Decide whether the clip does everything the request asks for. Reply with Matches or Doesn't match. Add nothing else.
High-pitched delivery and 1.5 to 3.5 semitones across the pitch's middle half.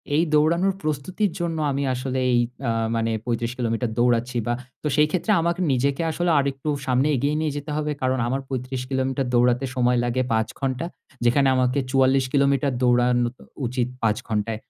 Doesn't match